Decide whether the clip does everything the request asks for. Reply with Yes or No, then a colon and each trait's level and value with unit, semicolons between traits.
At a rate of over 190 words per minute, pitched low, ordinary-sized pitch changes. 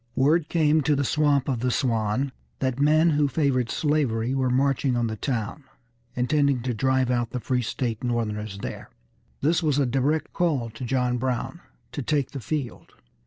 No: average, 175 wpm; low, 130 Hz; average, 3.3 semitones